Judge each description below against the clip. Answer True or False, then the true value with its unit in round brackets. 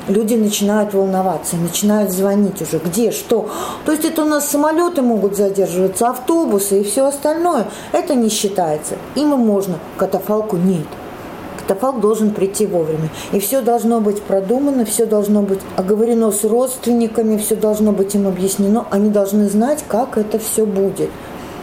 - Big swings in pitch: False (3.3 semitones)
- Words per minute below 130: False (155 wpm)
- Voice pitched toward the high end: True (210 Hz)